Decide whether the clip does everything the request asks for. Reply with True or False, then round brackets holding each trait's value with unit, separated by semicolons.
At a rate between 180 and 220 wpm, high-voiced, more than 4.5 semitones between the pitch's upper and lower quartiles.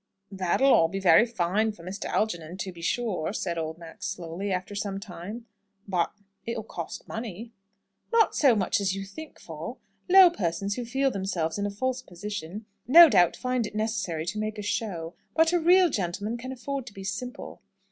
True (190 wpm; 205 Hz; 5.1 semitones)